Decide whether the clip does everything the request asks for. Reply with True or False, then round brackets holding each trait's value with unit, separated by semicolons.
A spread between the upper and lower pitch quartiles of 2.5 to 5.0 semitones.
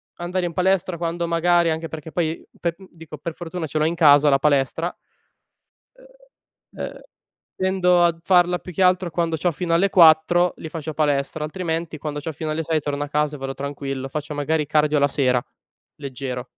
True (2.8 semitones)